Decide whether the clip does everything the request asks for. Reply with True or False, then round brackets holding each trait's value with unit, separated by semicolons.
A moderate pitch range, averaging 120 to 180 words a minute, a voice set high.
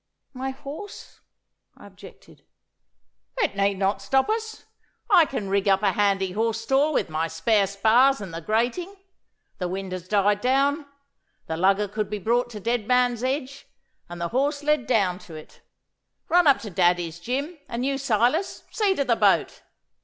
False (5.8 semitones; 170 wpm; 225 Hz)